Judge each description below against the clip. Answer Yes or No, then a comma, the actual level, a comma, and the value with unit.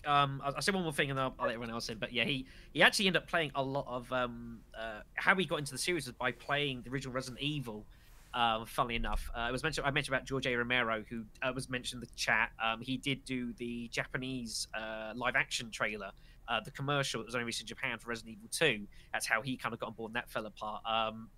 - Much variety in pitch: No, average, 3.1 semitones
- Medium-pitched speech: No, low, 125 Hz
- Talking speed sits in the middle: No, fast, 265 wpm